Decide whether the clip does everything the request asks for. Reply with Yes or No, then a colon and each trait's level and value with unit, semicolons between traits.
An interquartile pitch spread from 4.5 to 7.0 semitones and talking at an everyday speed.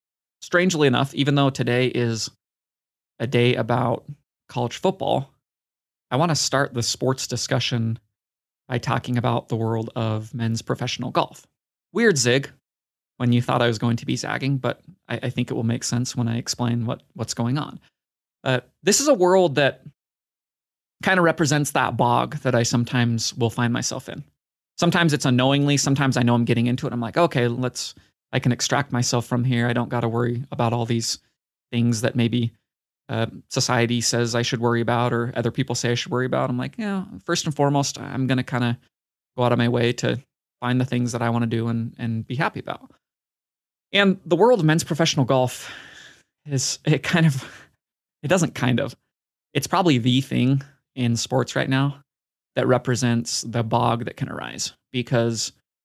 No: average, 2.7 semitones; average, 195 wpm